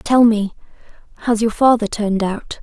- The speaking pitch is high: Yes, high, 220 Hz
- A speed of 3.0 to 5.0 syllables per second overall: Yes, 4.9 syllables/s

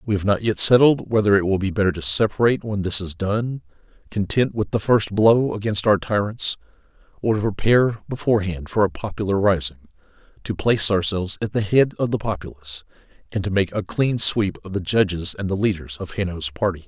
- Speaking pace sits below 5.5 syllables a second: No, 5.8 syllables/s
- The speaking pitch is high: No, low, 100 Hz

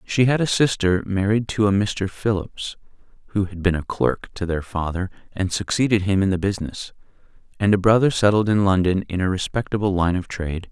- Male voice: Yes, male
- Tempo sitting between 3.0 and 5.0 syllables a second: No, 5.5 syllables/s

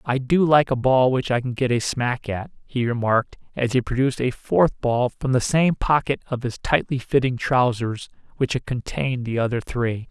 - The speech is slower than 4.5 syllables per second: No, 5.0 syllables/s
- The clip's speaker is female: No, male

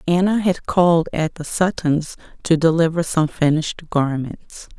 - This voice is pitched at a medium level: Yes, medium, 165 Hz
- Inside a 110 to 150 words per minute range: Yes, average, 140 wpm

